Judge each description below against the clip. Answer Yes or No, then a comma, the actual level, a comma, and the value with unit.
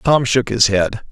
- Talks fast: Yes, fast, 215 wpm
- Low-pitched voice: Yes, low, 115 Hz